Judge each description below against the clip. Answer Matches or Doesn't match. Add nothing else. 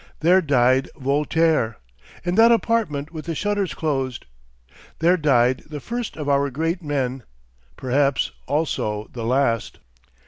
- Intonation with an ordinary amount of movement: Matches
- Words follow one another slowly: Matches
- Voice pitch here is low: Doesn't match